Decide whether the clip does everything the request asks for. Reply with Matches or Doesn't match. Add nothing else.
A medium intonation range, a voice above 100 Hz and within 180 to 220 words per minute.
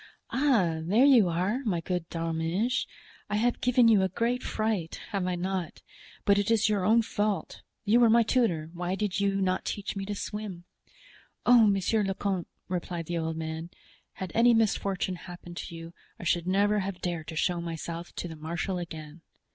Matches